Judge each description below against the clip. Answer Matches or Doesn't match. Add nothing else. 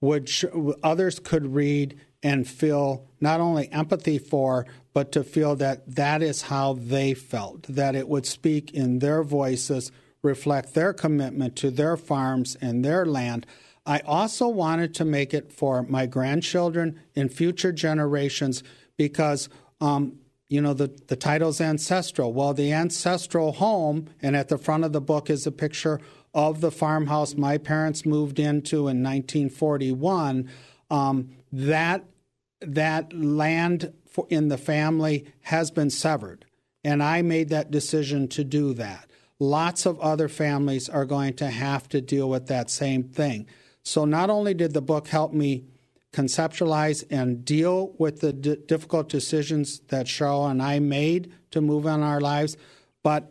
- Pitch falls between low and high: Matches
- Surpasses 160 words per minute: Doesn't match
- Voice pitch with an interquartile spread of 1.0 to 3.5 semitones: Matches